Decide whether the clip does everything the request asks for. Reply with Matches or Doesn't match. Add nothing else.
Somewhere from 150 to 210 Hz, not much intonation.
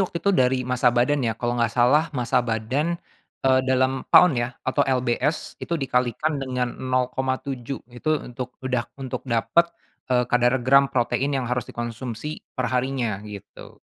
Doesn't match